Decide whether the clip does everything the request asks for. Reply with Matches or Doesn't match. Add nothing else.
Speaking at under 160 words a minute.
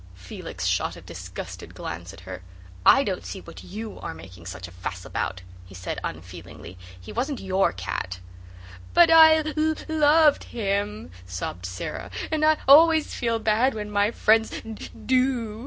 Doesn't match